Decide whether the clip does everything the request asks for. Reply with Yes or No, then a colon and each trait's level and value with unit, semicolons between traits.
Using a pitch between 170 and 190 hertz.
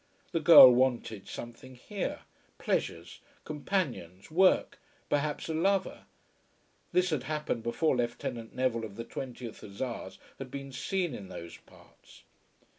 No: low, 130 Hz